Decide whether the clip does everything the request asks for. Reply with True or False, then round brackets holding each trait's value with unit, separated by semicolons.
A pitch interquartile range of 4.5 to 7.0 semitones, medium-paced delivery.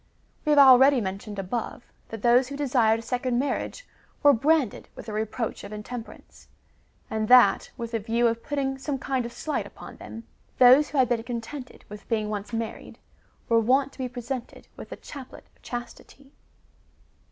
False (3.0 semitones; 185 wpm)